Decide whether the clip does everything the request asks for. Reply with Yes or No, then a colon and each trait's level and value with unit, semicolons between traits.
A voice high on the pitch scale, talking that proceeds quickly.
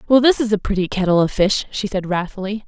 Yes: high, 200 Hz; fast, 245 wpm